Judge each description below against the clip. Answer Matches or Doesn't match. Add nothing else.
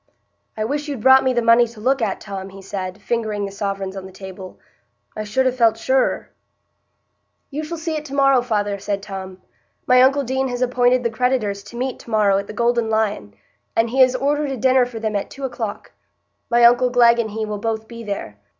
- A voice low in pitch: Doesn't match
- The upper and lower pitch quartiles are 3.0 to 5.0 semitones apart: Matches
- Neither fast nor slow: Doesn't match